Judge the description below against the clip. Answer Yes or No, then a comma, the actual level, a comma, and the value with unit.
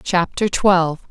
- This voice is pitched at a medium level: Yes, medium, 180 Hz